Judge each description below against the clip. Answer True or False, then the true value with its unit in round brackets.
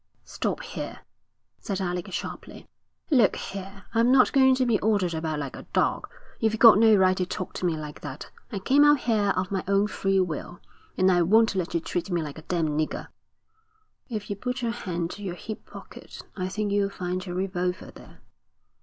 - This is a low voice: False (190 Hz)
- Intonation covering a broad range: False (3.6 semitones)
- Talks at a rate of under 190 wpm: False (200 wpm)